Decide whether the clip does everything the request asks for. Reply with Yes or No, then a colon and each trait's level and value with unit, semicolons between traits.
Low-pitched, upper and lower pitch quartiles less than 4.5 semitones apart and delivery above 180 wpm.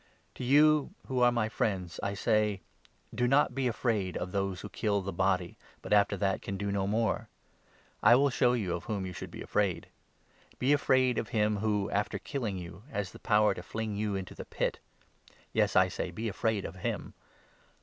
Yes: low, 105 Hz; average, 3.6 semitones; average, 200 wpm